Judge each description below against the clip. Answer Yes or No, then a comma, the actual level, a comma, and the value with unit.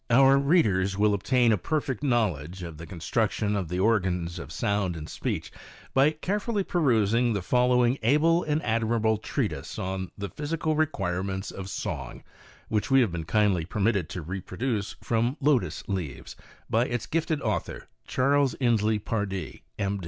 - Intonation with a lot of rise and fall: Yes, wide, 5.8 semitones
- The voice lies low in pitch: Yes, low, 110 Hz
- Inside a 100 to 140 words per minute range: No, average, 160 wpm